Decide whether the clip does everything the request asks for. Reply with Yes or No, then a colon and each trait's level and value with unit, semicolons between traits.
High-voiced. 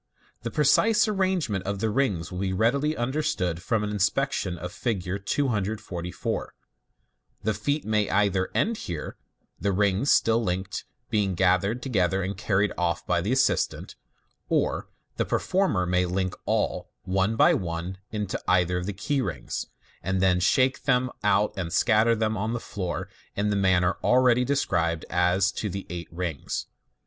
No: low, 100 Hz